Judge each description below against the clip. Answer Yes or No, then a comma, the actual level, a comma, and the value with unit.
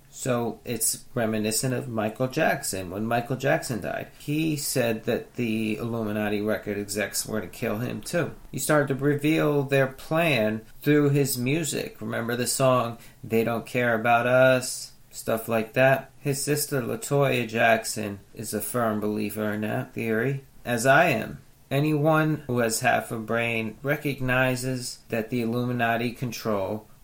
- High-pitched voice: No, low, 120 Hz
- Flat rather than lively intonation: No, average, 3.3 semitones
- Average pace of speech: Yes, average, 150 wpm